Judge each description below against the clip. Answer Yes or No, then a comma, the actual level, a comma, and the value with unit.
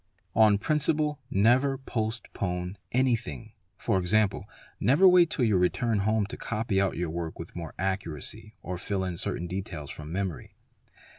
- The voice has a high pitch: No, low, 100 Hz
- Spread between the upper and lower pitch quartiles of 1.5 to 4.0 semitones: No, average, 4.9 semitones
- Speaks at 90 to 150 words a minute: Yes, average, 145 wpm